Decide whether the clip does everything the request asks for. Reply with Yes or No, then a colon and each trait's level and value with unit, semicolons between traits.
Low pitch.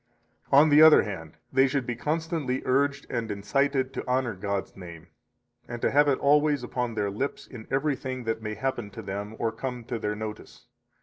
Yes: low, 125 Hz